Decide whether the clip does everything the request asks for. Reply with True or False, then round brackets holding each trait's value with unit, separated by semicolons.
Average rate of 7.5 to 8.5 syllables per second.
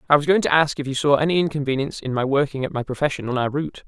True (7.7 syllables/s)